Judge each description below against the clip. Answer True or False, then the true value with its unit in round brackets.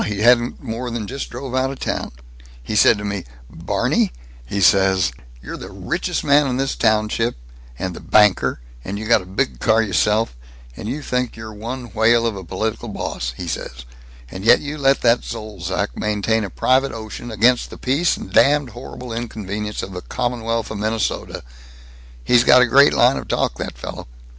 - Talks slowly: False (190 wpm)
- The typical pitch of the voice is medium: False (110 Hz)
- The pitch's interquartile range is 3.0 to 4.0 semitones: True (3.5 semitones)